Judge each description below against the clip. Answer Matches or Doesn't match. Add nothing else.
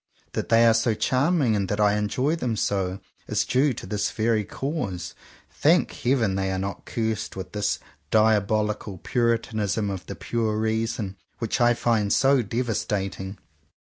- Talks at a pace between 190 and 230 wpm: Doesn't match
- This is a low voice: Matches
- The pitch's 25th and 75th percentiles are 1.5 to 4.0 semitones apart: Matches